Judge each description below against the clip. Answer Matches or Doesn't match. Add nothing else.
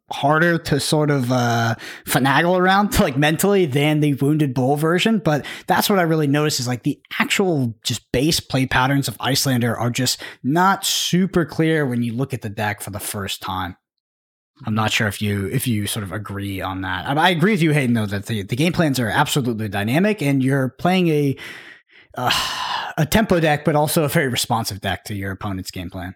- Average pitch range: Doesn't match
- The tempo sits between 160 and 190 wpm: Doesn't match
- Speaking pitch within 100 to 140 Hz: Matches